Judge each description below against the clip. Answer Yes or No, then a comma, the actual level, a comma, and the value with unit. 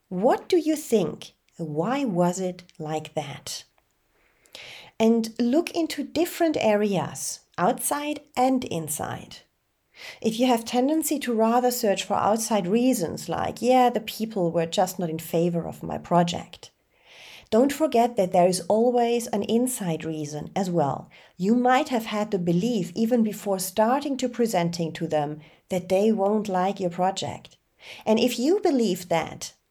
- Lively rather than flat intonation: Yes, wide, 5.7 semitones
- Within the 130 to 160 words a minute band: Yes, average, 150 wpm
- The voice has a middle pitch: No, high, 210 Hz